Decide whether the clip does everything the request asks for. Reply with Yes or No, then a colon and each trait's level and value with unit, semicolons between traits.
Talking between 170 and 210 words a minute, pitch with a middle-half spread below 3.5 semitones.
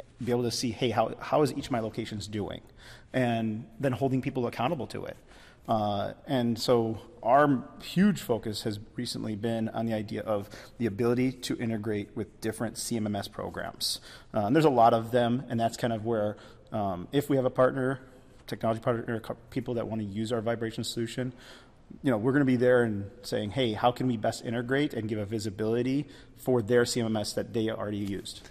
Yes: average, 200 wpm; narrow, 2.5 semitones